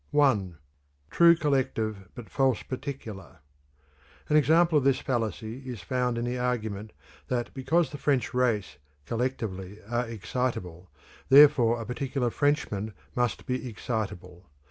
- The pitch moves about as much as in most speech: Yes, average, 3.8 semitones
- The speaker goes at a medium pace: No, slow, 125 wpm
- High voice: No, low, 125 Hz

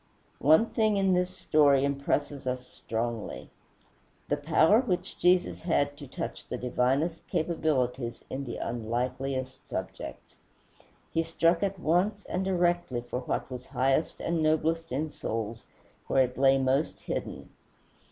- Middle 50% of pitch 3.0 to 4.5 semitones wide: No, average, 5.0 semitones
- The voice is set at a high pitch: No, medium, 145 Hz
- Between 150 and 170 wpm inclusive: No, slow, 135 wpm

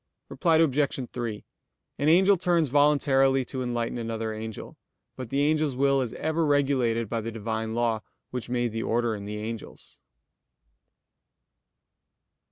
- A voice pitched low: Yes, low, 125 Hz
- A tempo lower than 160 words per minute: Yes, average, 140 wpm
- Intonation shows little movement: No, average, 4.1 semitones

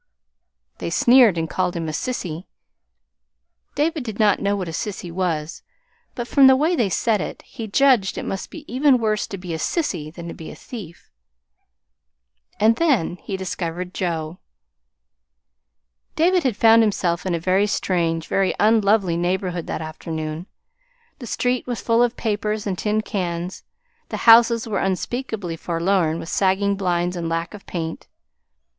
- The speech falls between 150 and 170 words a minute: Yes, average, 160 wpm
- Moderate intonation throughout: Yes, average, 5.0 semitones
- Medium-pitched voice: No, high, 195 Hz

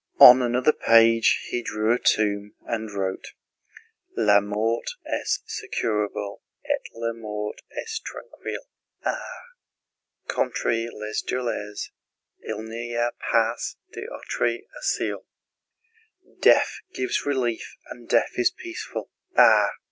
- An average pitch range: No, narrow, 2.3 semitones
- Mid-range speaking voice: No, low, 115 Hz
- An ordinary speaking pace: No, slow, 110 wpm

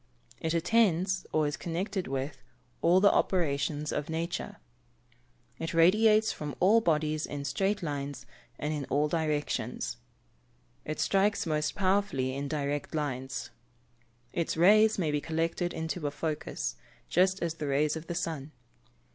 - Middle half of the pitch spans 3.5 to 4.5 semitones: Yes, average, 3.9 semitones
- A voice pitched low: No, medium, 160 Hz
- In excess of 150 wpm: No, average, 140 wpm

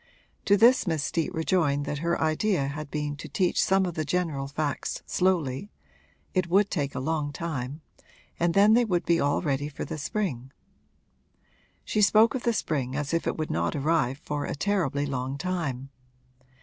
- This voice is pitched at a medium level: Yes, medium, 155 Hz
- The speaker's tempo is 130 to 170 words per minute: No, average, 180 wpm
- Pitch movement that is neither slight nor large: Yes, average, 4.5 semitones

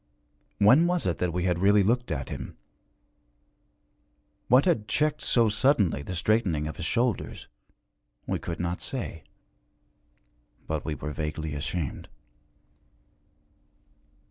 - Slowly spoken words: Yes, slow, 120 wpm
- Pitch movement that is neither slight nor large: No, wide, 7.0 semitones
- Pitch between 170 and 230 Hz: No, very low, 90 Hz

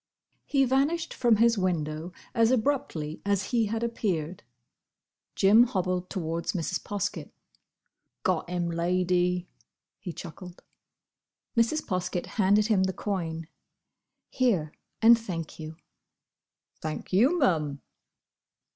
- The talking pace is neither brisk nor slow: No, slow, 110 wpm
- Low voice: No, medium, 185 Hz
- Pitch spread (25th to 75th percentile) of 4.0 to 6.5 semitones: Yes, average, 5.2 semitones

